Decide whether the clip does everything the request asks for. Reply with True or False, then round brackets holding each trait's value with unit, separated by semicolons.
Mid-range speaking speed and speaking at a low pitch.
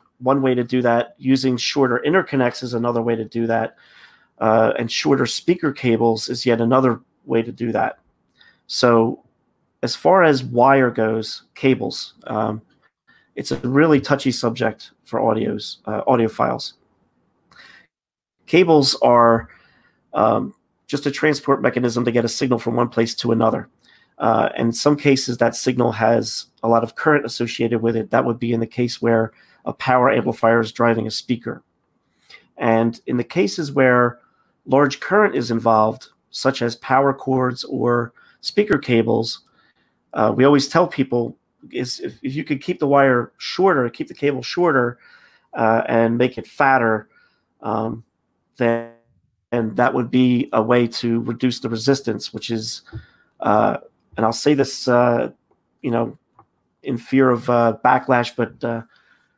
True (160 wpm; 120 Hz)